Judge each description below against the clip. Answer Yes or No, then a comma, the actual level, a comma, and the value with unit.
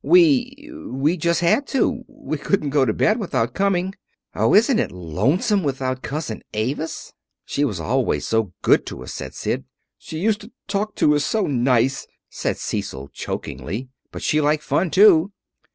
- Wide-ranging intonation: Yes, wide, 8.1 semitones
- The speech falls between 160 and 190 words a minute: Yes, average, 170 wpm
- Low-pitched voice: No, medium, 155 Hz